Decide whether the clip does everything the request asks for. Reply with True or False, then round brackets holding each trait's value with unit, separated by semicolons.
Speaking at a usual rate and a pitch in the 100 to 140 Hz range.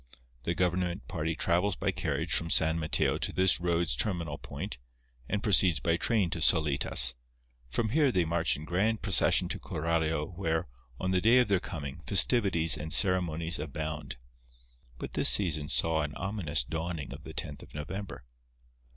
False (165 wpm; 85 Hz)